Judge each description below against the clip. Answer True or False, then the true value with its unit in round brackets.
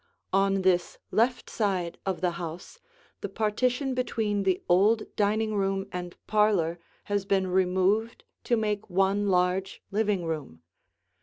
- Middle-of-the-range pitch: False (195 Hz)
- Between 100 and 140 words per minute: True (135 wpm)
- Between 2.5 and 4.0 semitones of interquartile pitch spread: True (2.9 semitones)